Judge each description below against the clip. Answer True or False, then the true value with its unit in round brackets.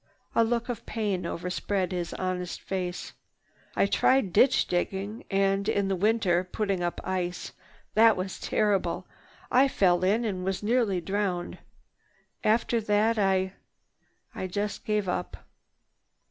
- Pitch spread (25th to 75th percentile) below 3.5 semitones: True (2.7 semitones)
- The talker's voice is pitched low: False (195 Hz)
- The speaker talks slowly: True (125 wpm)